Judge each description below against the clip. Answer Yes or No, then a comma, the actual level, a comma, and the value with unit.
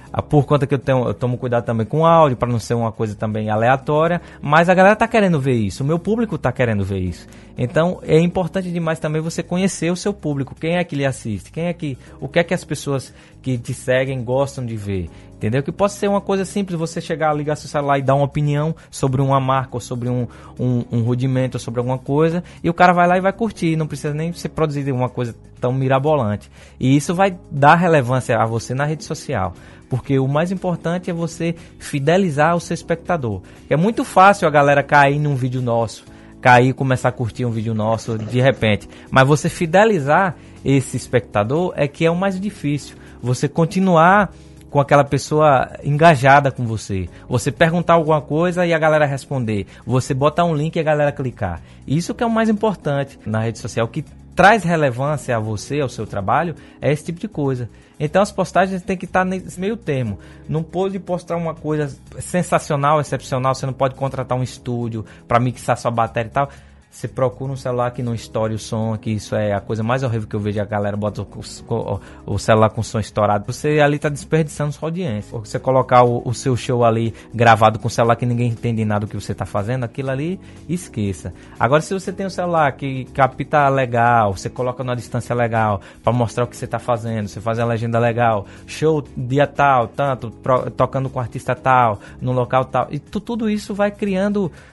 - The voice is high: No, low, 135 Hz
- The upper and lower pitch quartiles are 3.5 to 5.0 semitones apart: No, wide, 5.4 semitones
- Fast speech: Yes, fast, 215 wpm